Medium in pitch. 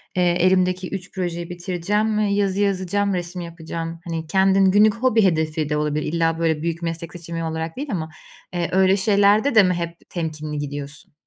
Yes: medium, 175 Hz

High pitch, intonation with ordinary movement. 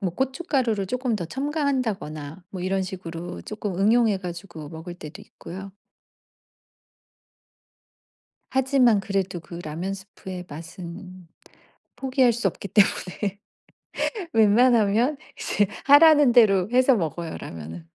No: high, 195 Hz; wide, 5.7 semitones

